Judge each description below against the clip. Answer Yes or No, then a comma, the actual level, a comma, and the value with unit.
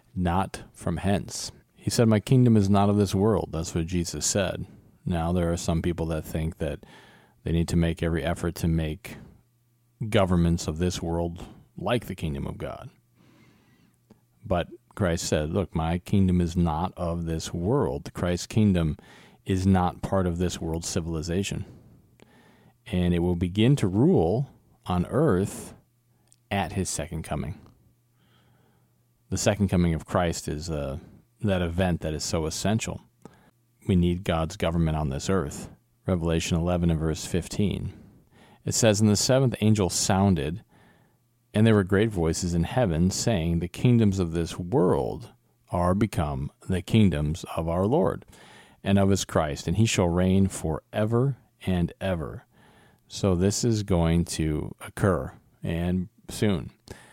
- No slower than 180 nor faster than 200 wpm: No, average, 150 wpm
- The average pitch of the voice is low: Yes, very low, 90 Hz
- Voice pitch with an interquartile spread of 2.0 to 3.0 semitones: No, average, 4.1 semitones